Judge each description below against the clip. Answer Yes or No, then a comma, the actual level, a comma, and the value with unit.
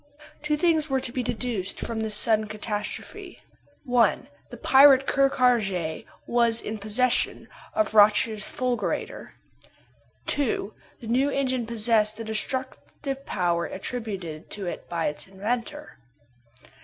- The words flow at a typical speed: No, slow, 125 wpm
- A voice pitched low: No, high, 230 Hz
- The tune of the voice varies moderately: Yes, average, 3.6 semitones